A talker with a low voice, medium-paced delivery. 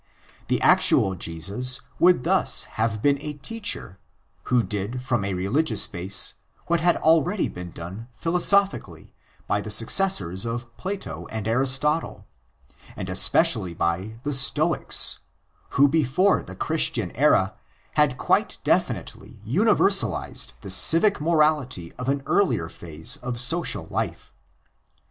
No: low, 125 Hz; slow, 130 wpm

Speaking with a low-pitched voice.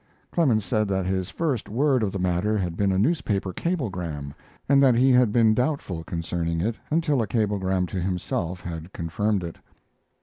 Yes: low, 100 Hz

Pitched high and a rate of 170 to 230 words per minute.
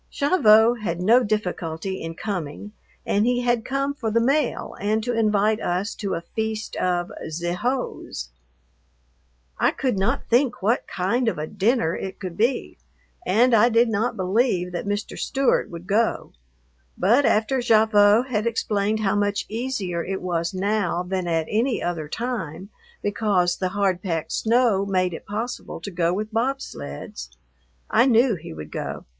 No: high, 210 Hz; average, 160 wpm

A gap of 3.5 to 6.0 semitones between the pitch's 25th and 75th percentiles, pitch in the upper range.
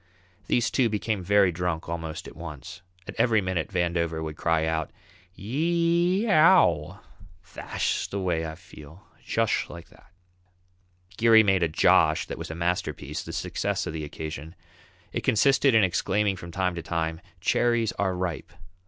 No: average, 5.1 semitones; very low, 90 Hz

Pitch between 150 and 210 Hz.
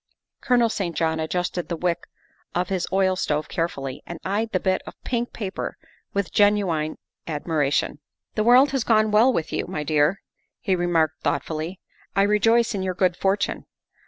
Yes: medium, 185 Hz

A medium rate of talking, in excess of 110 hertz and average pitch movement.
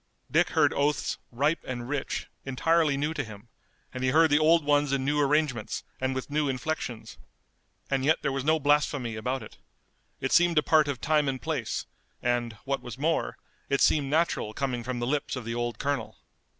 Yes: average, 195 wpm; medium, 140 Hz; average, 3.1 semitones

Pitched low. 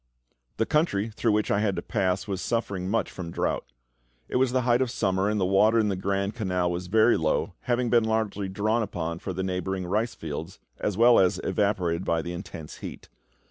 Yes: low, 100 Hz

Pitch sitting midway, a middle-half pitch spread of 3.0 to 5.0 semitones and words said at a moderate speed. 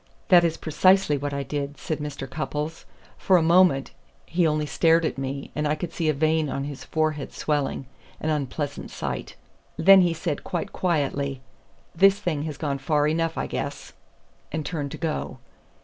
No: medium, 155 Hz; narrow, 2.5 semitones; average, 180 wpm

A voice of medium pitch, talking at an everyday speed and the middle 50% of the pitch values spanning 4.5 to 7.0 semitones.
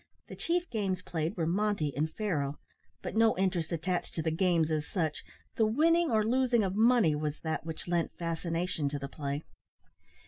Yes: medium, 175 Hz; average, 180 wpm; average, 5.3 semitones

